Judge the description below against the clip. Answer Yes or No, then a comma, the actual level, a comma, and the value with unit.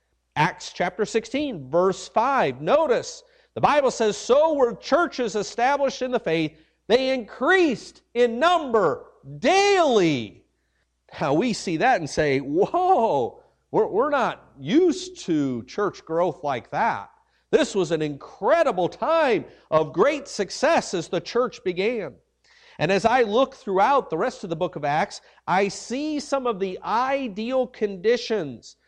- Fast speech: No, average, 140 wpm